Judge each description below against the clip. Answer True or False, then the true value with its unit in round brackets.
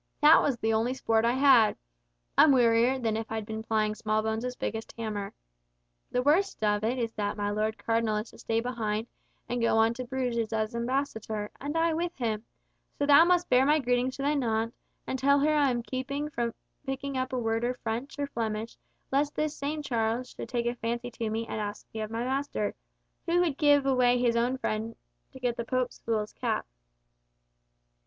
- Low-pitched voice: False (240 Hz)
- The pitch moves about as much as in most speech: True (3.4 semitones)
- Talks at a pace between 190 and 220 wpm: True (200 wpm)